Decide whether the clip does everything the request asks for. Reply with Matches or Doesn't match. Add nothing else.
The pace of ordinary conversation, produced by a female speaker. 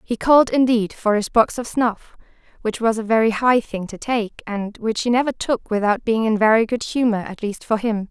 Doesn't match